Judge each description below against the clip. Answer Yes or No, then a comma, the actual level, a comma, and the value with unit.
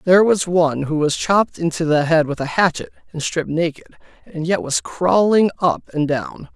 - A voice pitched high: No, medium, 165 Hz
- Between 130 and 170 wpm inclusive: No, average, 200 wpm